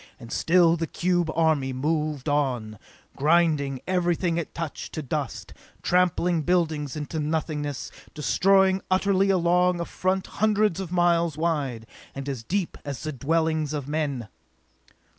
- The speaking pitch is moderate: Yes, medium, 160 Hz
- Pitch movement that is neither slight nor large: Yes, average, 3.5 semitones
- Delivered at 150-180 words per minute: No, slow, 135 wpm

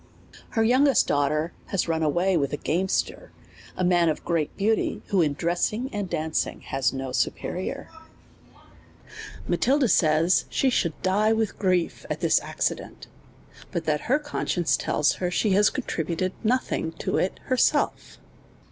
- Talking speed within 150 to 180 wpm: Yes, average, 155 wpm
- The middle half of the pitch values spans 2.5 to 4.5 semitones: No, average, 5.1 semitones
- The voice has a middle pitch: Yes, medium, 180 Hz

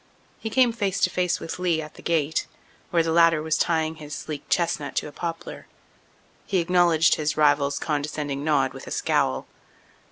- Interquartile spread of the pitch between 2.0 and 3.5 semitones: Yes, narrow, 2.5 semitones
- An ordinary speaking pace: Yes, average, 180 wpm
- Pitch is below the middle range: No, medium, 160 Hz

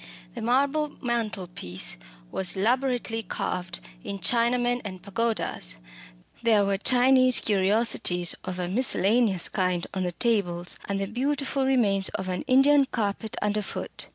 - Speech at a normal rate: No, slow, 125 wpm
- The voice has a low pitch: No, high, 215 Hz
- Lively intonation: No, average, 4.7 semitones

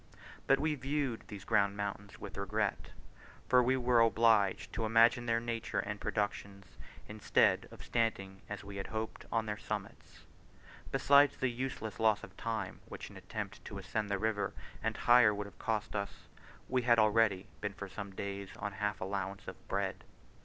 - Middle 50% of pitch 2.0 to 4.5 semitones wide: Yes, narrow, 2.6 semitones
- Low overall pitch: Yes, low, 110 Hz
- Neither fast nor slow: Yes, average, 175 wpm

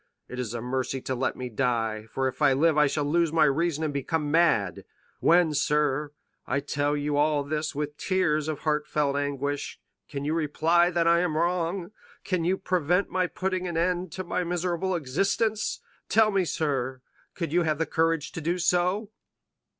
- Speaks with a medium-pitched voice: Yes, medium, 155 Hz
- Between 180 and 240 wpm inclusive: Yes, average, 185 wpm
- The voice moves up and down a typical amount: Yes, average, 3.5 semitones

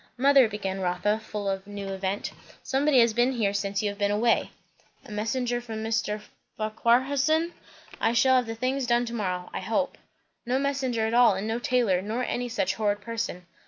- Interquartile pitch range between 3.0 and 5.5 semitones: Yes, average, 3.4 semitones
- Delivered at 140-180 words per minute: No, average, 195 wpm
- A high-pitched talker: Yes, high, 225 Hz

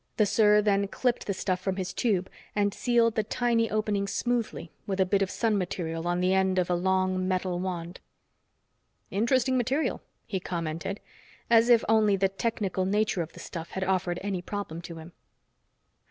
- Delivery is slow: No, average, 180 wpm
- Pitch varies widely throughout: No, average, 2.8 semitones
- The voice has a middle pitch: No, high, 195 Hz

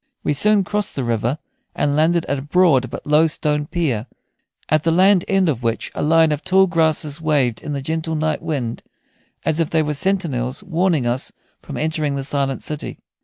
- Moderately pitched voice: Yes, medium, 155 Hz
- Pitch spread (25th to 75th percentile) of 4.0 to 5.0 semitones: No, average, 3.2 semitones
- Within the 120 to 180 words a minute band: No, average, 195 wpm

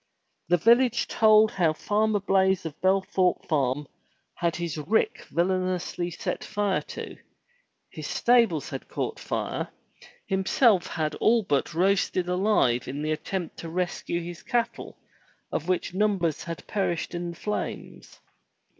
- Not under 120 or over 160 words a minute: Yes, slow, 135 wpm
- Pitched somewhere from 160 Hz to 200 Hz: Yes, medium, 185 Hz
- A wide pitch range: No, average, 3.6 semitones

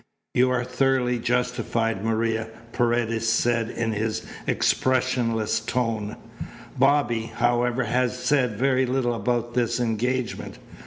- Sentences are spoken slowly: Yes, slow, 110 wpm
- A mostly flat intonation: Yes, narrow, 1.8 semitones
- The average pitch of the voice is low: Yes, low, 120 Hz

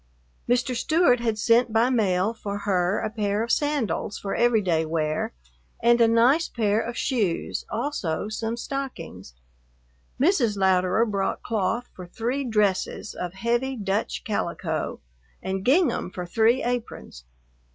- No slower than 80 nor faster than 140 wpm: Yes, slow, 135 wpm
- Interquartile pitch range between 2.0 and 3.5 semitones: No, average, 4.1 semitones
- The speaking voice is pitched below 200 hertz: No, high, 220 Hz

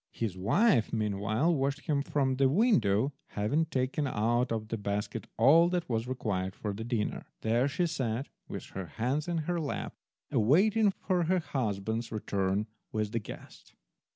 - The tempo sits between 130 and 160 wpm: Yes, average, 155 wpm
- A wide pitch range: Yes, wide, 6.1 semitones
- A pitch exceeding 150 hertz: No, low, 120 Hz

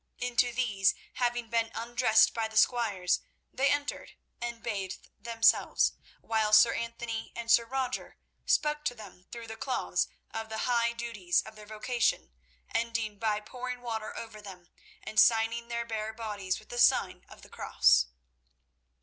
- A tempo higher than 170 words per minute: No, average, 155 wpm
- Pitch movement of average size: No, narrow, 1.8 semitones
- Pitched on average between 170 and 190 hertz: No, high, 230 Hz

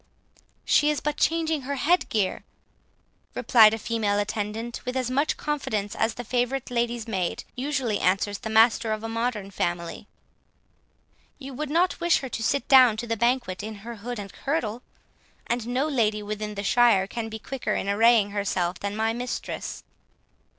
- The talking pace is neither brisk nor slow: Yes, average, 170 wpm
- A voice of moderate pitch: No, high, 230 Hz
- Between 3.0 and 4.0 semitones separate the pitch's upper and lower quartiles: Yes, average, 3.4 semitones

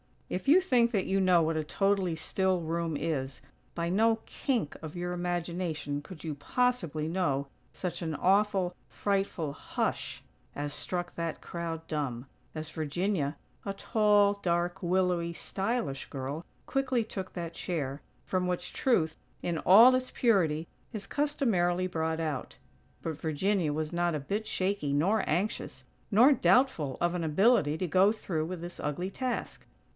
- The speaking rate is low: No, average, 150 wpm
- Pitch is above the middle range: No, medium, 175 Hz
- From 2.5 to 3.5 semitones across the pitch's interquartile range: No, average, 4.1 semitones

